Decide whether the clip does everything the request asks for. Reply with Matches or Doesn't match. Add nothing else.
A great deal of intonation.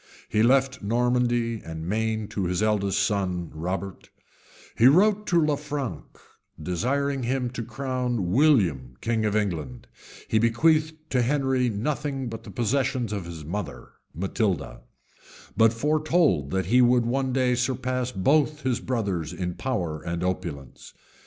Matches